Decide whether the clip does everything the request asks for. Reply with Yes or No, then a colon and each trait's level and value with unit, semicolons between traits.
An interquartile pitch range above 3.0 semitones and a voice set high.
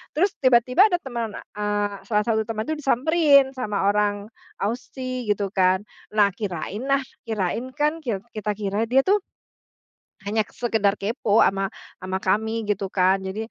Yes: average, 4.0 semitones; high, 220 Hz